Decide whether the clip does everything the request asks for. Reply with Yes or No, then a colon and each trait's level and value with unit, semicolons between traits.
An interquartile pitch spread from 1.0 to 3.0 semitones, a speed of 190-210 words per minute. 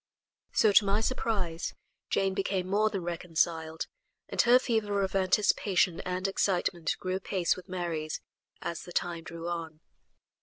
No: average, 2.7 semitones; average, 145 wpm